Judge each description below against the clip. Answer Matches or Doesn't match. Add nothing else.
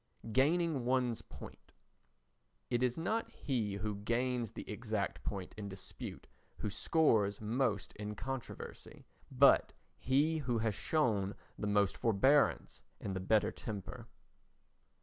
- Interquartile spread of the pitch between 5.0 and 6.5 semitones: Doesn't match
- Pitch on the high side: Doesn't match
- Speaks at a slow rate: Matches